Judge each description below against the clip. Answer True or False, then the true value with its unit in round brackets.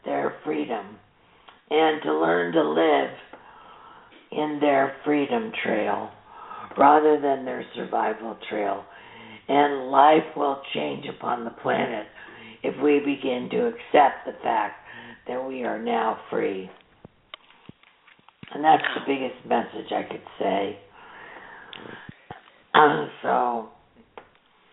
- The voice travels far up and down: True (6.3 semitones)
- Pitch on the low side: False (145 Hz)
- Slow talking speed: True (110 wpm)